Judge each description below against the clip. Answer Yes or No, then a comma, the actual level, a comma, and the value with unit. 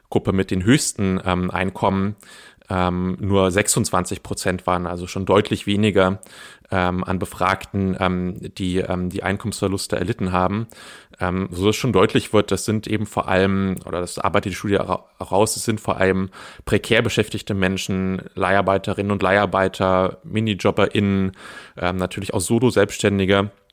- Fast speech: No, average, 145 wpm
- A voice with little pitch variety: Yes, narrow, 1.8 semitones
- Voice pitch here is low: Yes, very low, 95 Hz